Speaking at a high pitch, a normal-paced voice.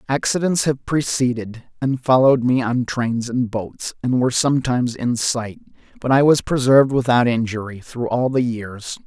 No: low, 125 Hz; average, 165 wpm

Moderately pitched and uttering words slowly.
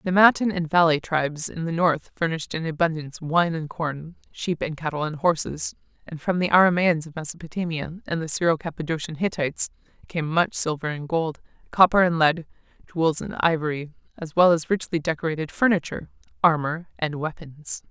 No: medium, 165 Hz; average, 170 wpm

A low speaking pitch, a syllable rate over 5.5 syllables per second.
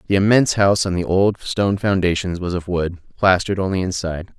Yes: very low, 95 Hz; 6.4 syllables/s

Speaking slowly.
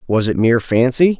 No: average, 200 wpm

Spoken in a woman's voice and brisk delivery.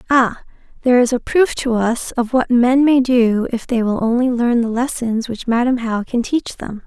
Yes: female; fast, 220 wpm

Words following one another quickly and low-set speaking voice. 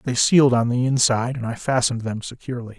Yes: fast, 215 wpm; low, 120 Hz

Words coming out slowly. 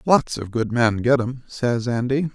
No: fast, 205 wpm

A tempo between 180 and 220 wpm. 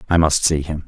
No: fast, 275 wpm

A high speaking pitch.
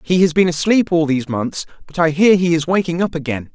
No: medium, 165 Hz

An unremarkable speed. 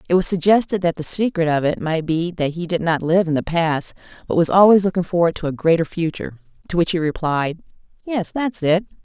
No: fast, 225 wpm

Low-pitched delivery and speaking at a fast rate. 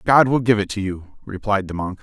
Yes: low, 105 Hz; fast, 265 wpm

